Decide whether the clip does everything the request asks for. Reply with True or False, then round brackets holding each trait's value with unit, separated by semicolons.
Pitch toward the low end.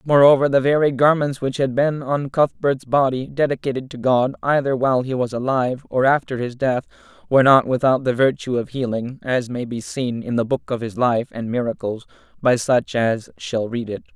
True (130 Hz)